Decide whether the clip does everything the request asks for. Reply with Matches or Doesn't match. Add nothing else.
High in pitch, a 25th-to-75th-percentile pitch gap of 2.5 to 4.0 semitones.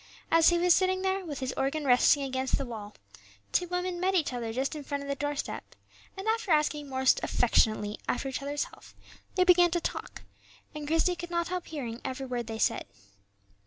Doesn't match